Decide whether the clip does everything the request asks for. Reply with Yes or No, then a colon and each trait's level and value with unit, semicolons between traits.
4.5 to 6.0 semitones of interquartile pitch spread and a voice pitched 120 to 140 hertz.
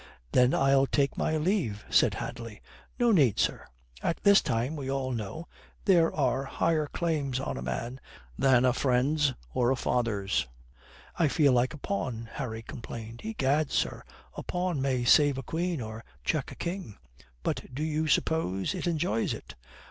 Yes: average, 4.9 semitones; low, 135 Hz